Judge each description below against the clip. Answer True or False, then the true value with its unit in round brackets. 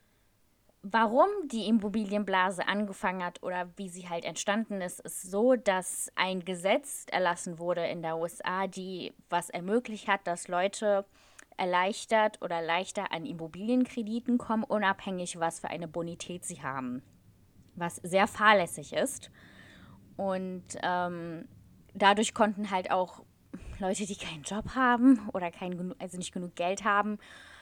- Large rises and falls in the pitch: False (3.2 semitones)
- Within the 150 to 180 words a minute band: False (135 wpm)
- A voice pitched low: False (185 Hz)